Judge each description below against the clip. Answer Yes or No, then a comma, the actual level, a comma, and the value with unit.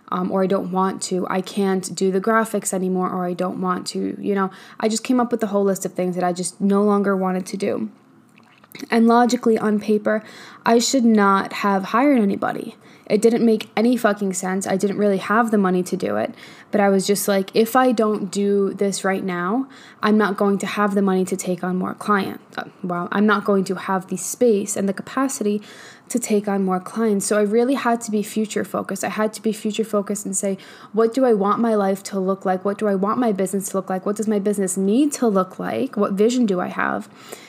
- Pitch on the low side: No, high, 205 Hz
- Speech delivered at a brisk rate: Yes, fast, 240 wpm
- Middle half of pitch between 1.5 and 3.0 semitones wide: Yes, narrow, 2.5 semitones